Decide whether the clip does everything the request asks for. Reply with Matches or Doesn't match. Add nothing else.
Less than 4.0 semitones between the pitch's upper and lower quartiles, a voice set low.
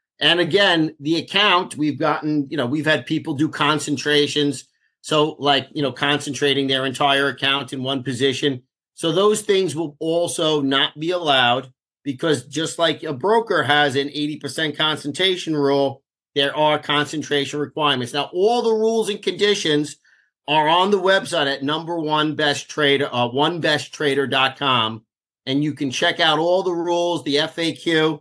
Doesn't match